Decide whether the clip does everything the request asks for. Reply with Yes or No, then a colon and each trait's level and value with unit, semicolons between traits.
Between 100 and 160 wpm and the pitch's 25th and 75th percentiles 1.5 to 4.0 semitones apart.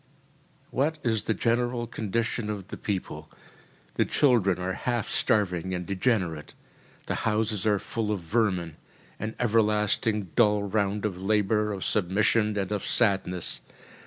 Yes: slow, 135 wpm; average, 2.8 semitones